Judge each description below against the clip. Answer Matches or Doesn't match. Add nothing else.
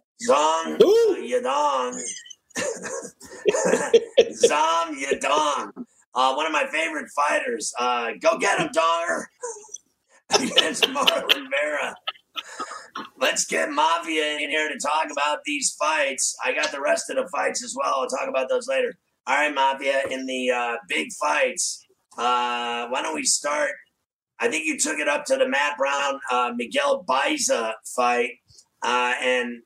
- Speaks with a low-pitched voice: Doesn't match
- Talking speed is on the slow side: Doesn't match